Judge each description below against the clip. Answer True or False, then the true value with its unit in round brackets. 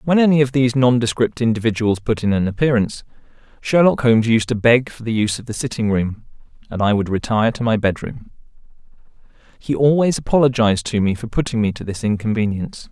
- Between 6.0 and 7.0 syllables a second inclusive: True (6.3 syllables/s)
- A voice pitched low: True (115 Hz)